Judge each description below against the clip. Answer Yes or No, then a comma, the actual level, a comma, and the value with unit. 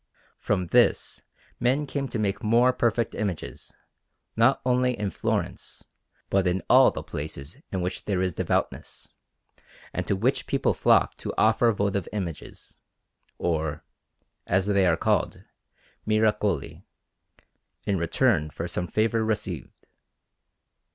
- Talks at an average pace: No, slow, 125 wpm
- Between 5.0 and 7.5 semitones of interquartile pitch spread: No, average, 4.3 semitones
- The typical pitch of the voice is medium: No, low, 100 Hz